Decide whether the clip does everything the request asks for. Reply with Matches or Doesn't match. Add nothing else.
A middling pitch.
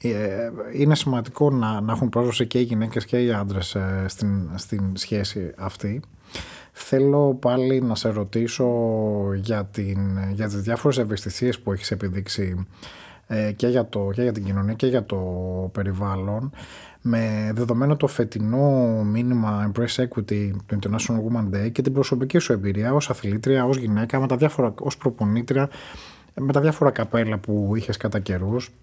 Doesn't match